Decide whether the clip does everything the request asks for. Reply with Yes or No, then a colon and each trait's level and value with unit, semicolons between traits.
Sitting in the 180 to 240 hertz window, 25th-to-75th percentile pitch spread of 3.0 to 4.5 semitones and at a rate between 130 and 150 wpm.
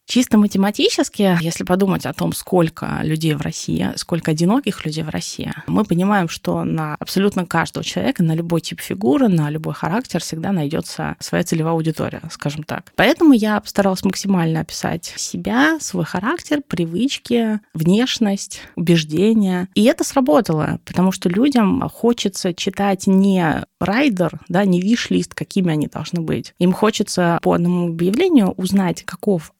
Yes: medium, 185 Hz; average, 4.2 semitones; average, 145 wpm